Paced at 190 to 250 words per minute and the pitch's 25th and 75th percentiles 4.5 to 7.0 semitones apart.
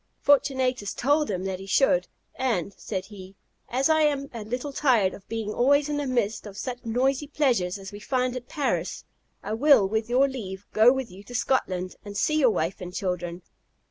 Yes: average, 200 wpm; wide, 5.6 semitones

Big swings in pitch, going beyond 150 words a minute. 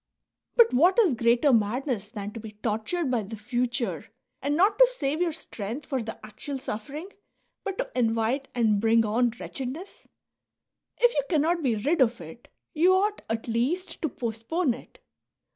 Yes: wide, 6.4 semitones; average, 170 wpm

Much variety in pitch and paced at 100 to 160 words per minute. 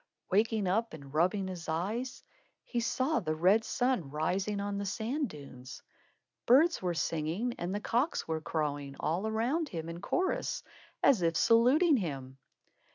Yes: wide, 6.7 semitones; average, 155 wpm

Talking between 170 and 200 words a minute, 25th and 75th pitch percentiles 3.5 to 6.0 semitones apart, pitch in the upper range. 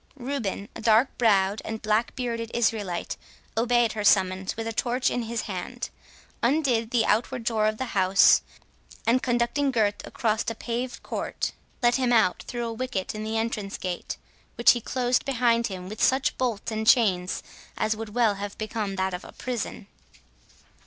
No: average, 175 wpm; narrow, 2.6 semitones; high, 225 Hz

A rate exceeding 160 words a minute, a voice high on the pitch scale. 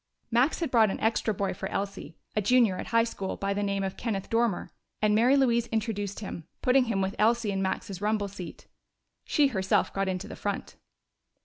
Yes: average, 200 wpm; high, 210 Hz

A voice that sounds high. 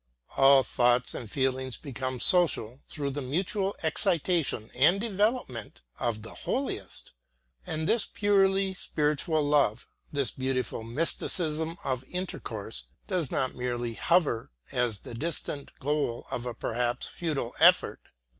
No: medium, 140 Hz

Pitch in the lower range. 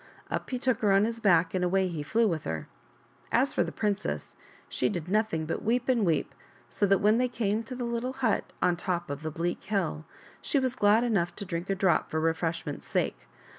No: high, 200 Hz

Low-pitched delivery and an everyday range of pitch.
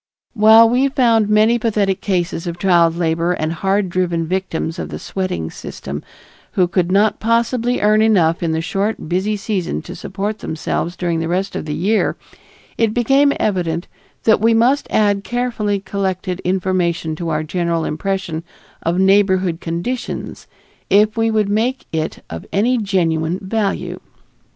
No: high, 190 Hz; average, 4.2 semitones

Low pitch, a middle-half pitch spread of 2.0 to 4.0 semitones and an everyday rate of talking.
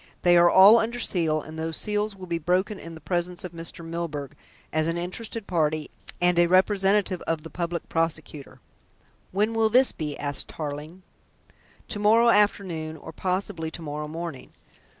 No: medium, 175 Hz; average, 3.7 semitones; average, 170 wpm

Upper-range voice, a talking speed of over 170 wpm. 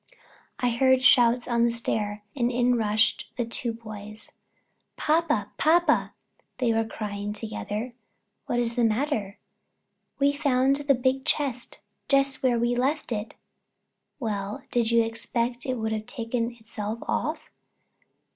No: high, 235 Hz; slow, 135 wpm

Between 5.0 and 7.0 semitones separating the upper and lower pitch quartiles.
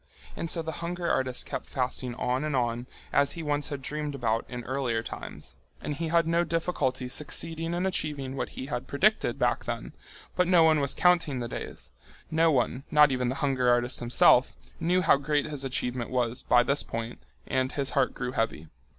No: average, 4.3 semitones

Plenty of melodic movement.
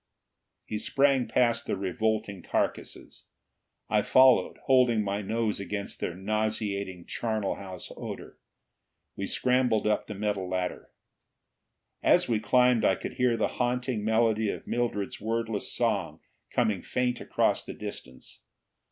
No: average, 3.4 semitones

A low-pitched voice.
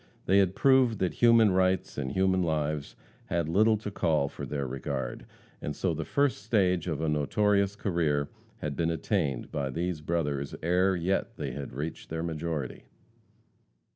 Yes: very low, 85 Hz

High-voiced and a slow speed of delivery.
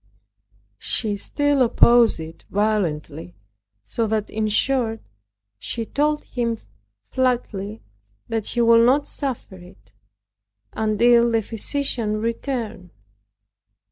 Yes: high, 225 Hz; slow, 100 wpm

